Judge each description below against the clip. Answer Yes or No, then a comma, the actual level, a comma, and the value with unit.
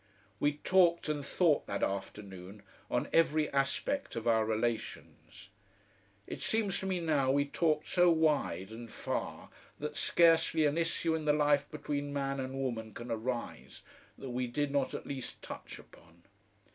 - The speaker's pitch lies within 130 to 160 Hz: Yes, medium, 140 Hz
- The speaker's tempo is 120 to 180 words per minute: Yes, average, 160 wpm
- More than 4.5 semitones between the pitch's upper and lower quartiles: Yes, average, 5.3 semitones